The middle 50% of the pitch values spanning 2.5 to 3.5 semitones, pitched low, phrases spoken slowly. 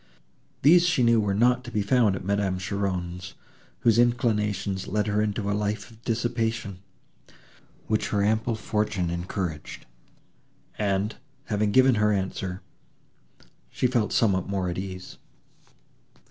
Yes: average, 3.0 semitones; low, 105 Hz; slow, 130 wpm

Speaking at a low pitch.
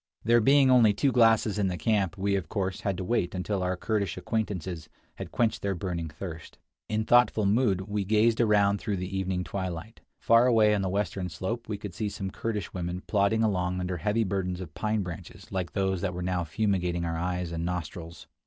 Yes: very low, 95 Hz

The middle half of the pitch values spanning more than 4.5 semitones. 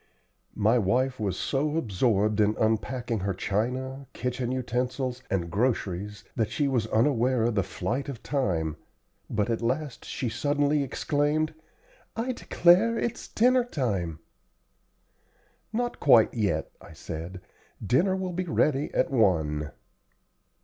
Yes: wide, 5.6 semitones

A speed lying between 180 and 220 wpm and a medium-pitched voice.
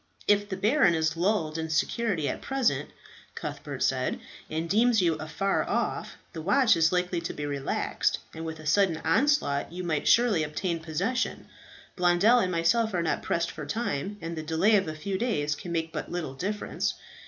Yes: average, 185 wpm; medium, 175 Hz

